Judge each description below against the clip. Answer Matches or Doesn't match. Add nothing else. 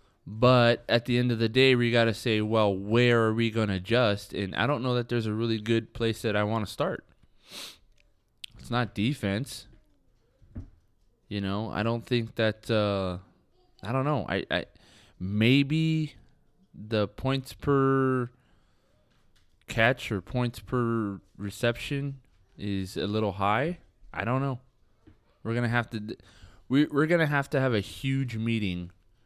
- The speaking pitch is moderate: Doesn't match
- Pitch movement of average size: Matches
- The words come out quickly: Doesn't match